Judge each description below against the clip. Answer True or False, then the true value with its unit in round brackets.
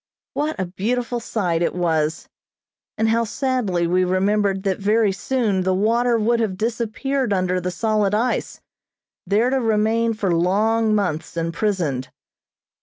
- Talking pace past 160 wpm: False (140 wpm)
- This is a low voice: False (210 Hz)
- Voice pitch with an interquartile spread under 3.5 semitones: False (3.9 semitones)